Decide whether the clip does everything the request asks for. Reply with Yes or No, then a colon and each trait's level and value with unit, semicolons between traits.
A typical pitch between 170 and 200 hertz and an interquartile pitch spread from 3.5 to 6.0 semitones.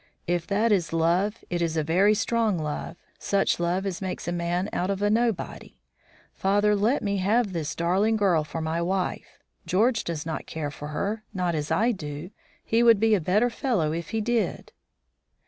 Yes: medium, 185 Hz; average, 4.1 semitones